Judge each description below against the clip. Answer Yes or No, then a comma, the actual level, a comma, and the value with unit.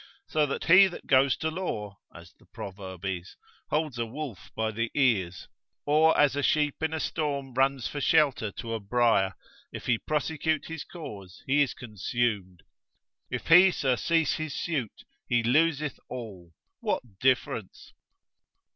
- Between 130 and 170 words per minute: Yes, average, 155 wpm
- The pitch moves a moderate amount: No, wide, 6.2 semitones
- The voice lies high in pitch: No, low, 130 Hz